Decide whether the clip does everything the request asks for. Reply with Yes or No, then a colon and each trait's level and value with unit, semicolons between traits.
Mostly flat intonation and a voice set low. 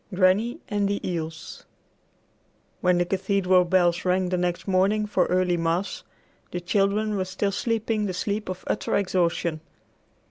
No: narrow, 2.2 semitones; medium, 185 Hz